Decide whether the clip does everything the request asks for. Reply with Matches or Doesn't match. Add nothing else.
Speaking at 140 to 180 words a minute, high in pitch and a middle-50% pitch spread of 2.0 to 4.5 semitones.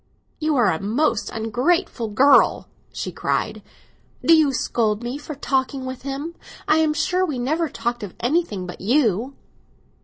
Doesn't match